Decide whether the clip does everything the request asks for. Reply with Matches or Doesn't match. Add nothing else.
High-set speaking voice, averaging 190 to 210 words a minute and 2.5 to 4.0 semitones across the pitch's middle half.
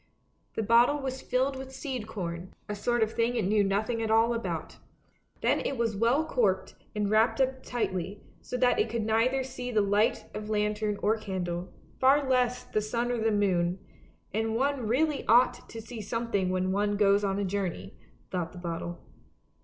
Matches